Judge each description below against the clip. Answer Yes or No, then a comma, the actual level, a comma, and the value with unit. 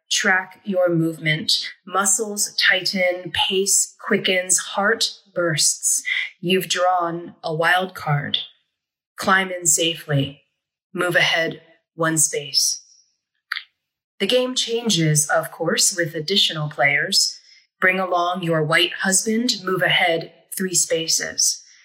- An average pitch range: Yes, average, 3.1 semitones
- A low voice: No, medium, 180 Hz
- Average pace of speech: No, slow, 105 wpm